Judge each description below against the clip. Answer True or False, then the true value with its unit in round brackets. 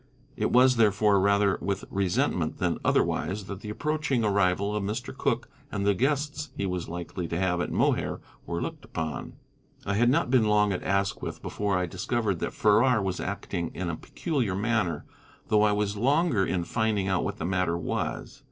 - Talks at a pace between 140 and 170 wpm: False (185 wpm)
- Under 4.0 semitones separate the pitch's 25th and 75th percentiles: True (3.6 semitones)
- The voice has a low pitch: True (100 Hz)